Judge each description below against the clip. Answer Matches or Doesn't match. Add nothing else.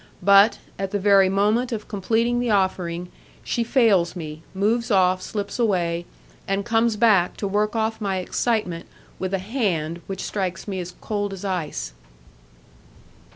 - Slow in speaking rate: Doesn't match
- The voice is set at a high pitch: Matches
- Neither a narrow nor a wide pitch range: Matches